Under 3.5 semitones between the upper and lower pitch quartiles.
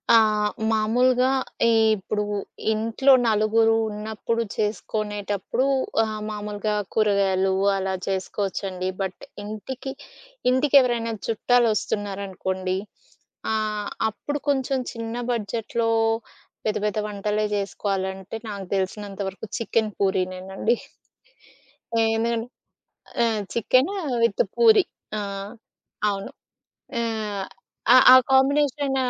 Yes: average, 2.8 semitones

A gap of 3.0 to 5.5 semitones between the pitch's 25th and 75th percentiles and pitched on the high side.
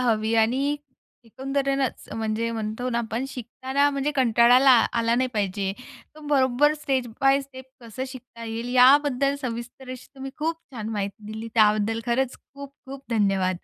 Yes: average, 3.3 semitones; high, 245 Hz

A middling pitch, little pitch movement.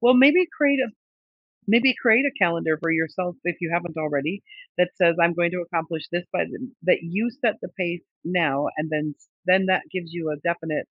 No: medium, 175 Hz; average, 3.6 semitones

